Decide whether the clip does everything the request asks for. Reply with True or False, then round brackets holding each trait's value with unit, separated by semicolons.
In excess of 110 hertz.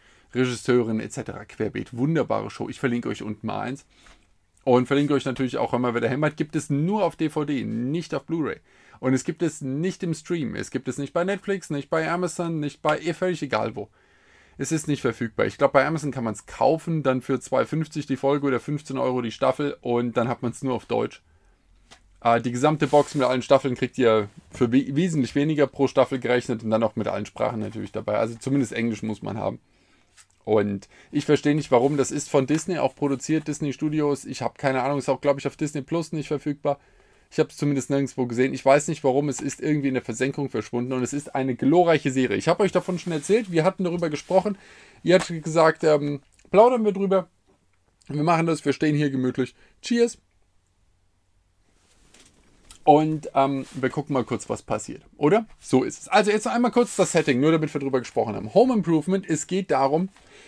True (140 Hz)